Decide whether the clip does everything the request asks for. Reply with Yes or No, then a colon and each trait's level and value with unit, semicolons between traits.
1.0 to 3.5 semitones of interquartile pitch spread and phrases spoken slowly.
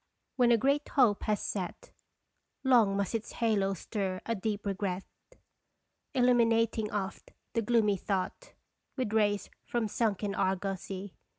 Yes: average, 2.8 semitones; slow, 125 wpm